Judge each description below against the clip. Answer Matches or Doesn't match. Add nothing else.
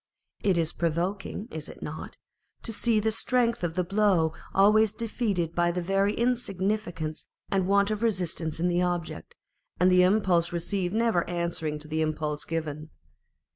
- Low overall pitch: Doesn't match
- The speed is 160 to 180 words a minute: Matches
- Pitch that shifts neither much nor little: Matches